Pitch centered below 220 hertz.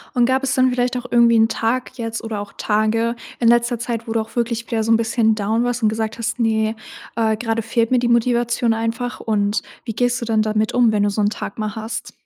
No: high, 230 Hz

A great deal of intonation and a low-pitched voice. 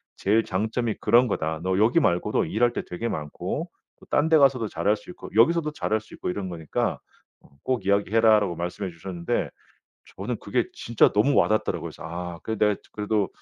No: average, 4.5 semitones; low, 105 Hz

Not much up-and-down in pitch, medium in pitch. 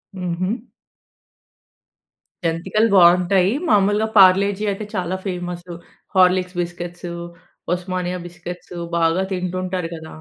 Yes: narrow, 1.4 semitones; medium, 180 Hz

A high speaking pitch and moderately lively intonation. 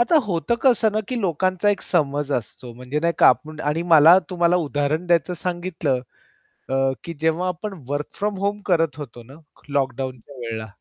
No: medium, 160 Hz; average, 4.7 semitones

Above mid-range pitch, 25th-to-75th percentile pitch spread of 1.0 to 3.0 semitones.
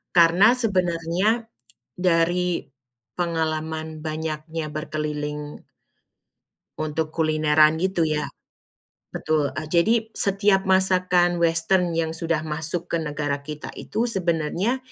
No: medium, 165 Hz; average, 2.7 semitones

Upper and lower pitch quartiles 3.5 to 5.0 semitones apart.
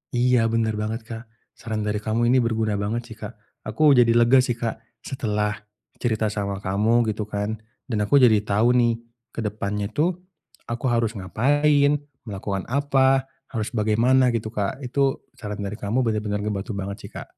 No: average, 2.7 semitones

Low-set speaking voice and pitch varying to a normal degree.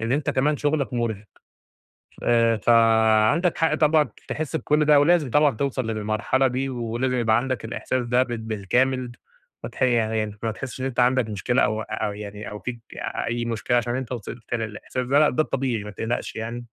Yes: low, 120 Hz; average, 3.0 semitones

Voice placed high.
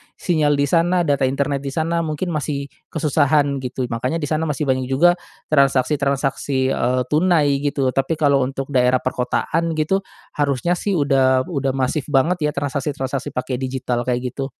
No: medium, 140 Hz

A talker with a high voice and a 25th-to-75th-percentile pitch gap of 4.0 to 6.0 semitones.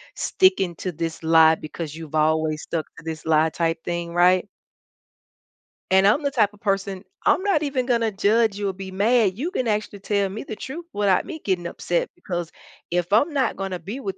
Yes: high, 195 Hz; average, 4.7 semitones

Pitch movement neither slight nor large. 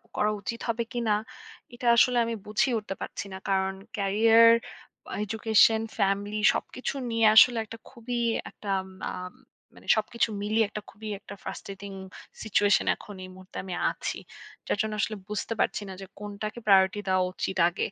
No: narrow, 2.3 semitones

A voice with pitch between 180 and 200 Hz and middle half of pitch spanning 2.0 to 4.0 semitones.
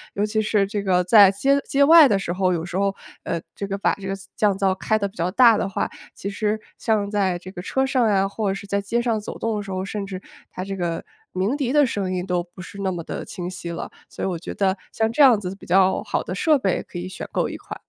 Yes: high, 195 Hz; average, 2.7 semitones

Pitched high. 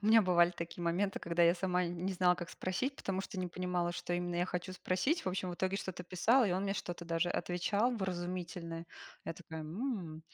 No: medium, 180 Hz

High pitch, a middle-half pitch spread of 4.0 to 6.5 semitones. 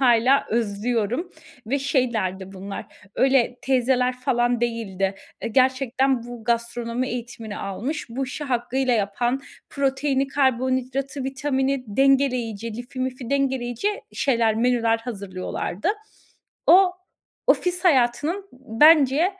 No: very high, 250 Hz; average, 2.7 semitones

